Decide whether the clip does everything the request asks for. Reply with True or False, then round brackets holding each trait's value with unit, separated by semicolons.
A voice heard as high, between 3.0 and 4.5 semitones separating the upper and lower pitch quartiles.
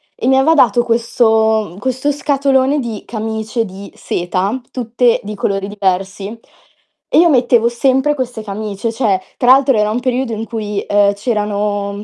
True (225 Hz; 3.8 semitones)